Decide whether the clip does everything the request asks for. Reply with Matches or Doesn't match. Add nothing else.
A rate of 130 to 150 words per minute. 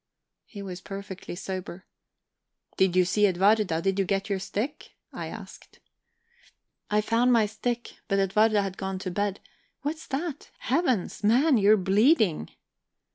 Matches